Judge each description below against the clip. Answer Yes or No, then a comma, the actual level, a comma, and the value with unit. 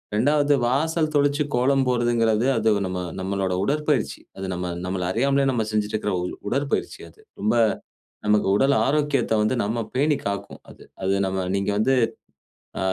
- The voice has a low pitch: Yes, low, 120 Hz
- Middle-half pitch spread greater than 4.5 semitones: Yes, average, 5.3 semitones